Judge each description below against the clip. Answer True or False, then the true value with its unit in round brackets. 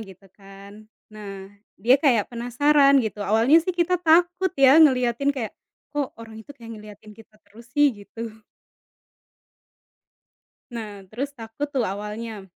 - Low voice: False (230 Hz)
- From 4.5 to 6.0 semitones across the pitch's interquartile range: True (5.0 semitones)